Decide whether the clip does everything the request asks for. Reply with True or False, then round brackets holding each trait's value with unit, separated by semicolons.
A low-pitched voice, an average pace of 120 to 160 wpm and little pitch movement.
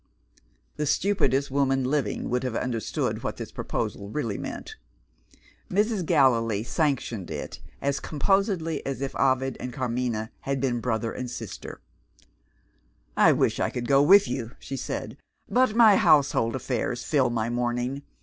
False (130 Hz; 145 wpm; 3.4 semitones)